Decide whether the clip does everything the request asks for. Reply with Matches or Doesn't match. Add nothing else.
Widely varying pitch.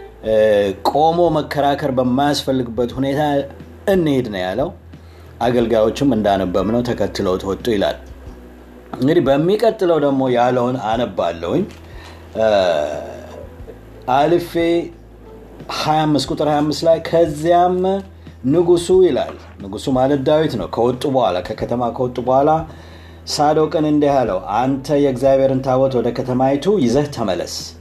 Matches